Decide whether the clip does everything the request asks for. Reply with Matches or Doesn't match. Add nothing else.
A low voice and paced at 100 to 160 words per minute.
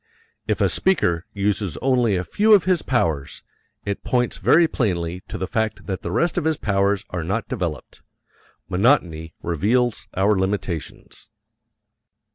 Matches